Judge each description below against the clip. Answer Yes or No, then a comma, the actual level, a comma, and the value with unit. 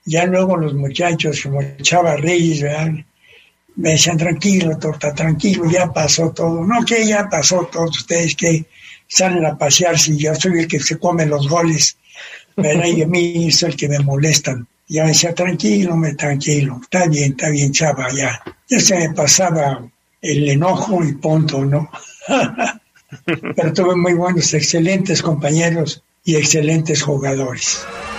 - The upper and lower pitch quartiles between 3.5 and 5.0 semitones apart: No, average, 2.7 semitones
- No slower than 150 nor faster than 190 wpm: Yes, average, 155 wpm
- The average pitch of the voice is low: No, medium, 160 Hz